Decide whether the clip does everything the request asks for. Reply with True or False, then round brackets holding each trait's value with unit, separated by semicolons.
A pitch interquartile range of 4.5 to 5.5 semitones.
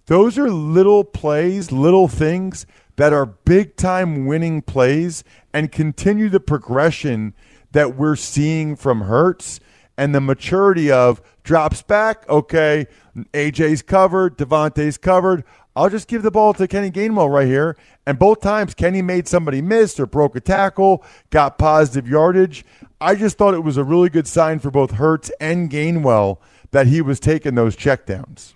True (5.0 semitones)